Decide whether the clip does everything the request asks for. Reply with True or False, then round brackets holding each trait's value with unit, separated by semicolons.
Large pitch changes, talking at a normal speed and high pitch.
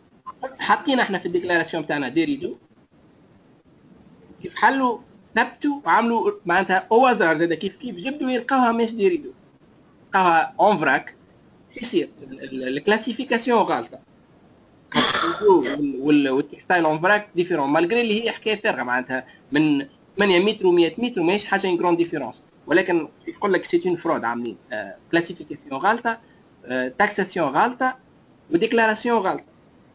False (6.2 semitones; 120 wpm; 210 Hz)